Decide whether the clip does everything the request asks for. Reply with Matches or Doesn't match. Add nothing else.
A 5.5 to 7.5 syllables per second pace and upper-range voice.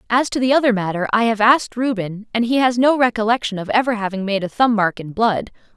Matches